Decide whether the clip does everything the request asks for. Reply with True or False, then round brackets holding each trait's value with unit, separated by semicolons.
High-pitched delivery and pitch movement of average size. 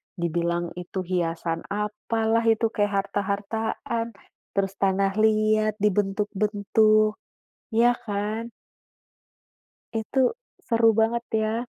False (210 Hz; 2.3 semitones)